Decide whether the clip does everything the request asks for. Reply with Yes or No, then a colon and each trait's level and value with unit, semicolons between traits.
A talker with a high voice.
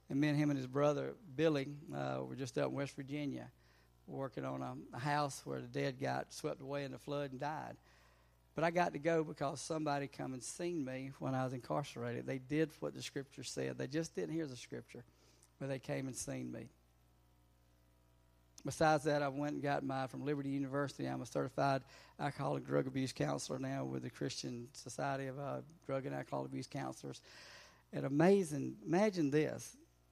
No: low, 135 Hz